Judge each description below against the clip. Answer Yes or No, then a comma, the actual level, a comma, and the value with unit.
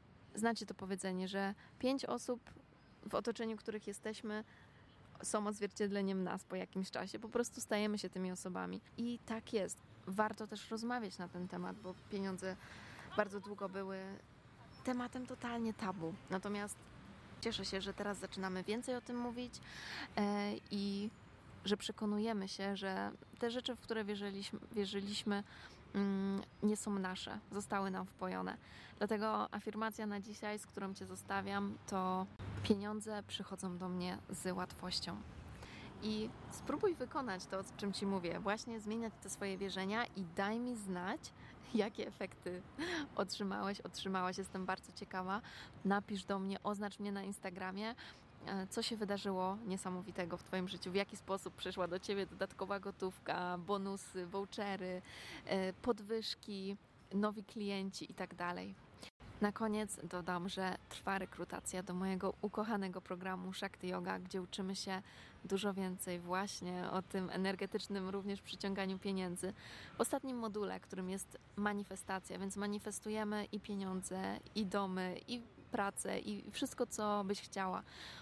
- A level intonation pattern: Yes, narrow, 2.1 semitones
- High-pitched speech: Yes, high, 200 Hz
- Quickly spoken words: No, average, 135 wpm